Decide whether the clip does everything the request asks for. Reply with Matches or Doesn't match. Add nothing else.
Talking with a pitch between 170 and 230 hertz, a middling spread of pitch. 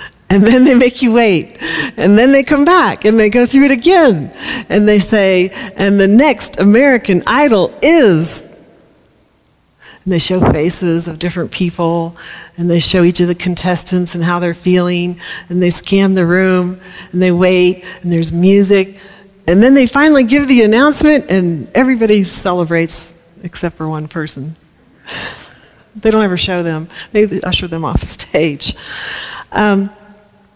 Matches